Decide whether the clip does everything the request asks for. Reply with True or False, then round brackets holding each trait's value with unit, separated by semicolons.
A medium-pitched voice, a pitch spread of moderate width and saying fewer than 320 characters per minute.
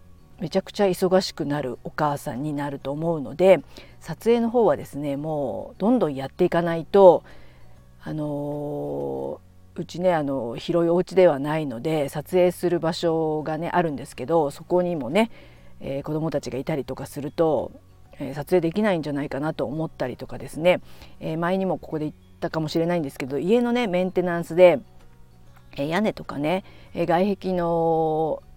False (160 Hz; 4.3 semitones; 340 characters per minute)